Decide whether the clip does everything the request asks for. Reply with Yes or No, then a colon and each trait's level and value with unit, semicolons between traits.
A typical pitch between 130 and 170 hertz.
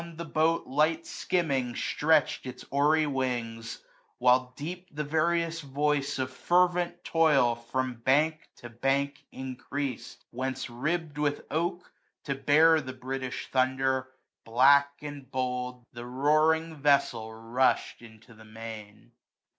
Yes: medium, 140 Hz